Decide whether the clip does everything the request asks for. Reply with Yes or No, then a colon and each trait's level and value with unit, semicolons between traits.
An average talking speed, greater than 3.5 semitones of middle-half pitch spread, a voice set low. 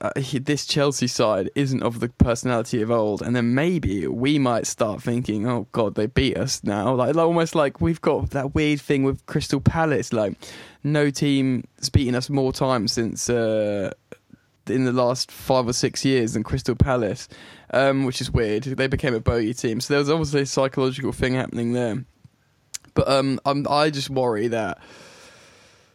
No: average, 185 wpm; average, 3.0 semitones; low, 130 Hz